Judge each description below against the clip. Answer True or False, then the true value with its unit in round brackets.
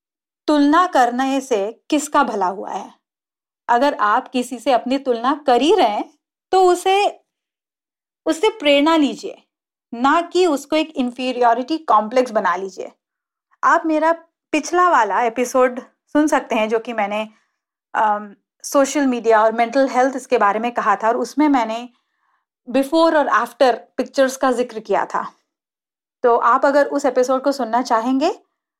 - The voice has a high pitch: True (270 Hz)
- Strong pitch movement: False (4.5 semitones)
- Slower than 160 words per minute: True (150 wpm)